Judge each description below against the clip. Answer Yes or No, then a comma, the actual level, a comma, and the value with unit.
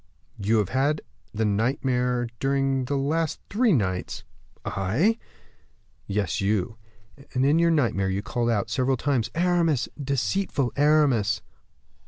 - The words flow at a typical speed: No, slow, 125 wpm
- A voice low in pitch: Yes, low, 130 Hz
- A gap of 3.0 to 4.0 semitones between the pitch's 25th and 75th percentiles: No, average, 5.3 semitones